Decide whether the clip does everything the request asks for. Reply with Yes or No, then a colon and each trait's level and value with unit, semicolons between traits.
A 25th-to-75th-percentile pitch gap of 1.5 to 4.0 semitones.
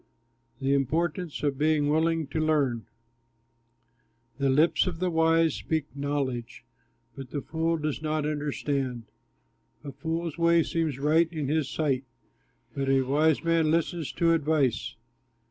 Yes: average, 2.9 semitones